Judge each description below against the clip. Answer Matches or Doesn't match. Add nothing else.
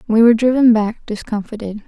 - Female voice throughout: Matches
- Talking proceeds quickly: Doesn't match